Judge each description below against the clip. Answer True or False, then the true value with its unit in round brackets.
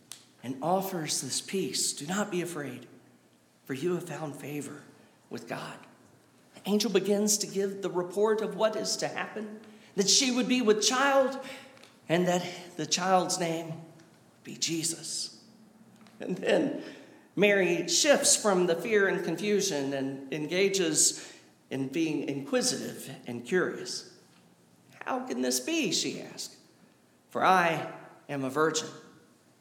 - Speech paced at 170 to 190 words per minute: False (140 wpm)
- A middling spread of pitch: False (6.5 semitones)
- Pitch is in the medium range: True (180 Hz)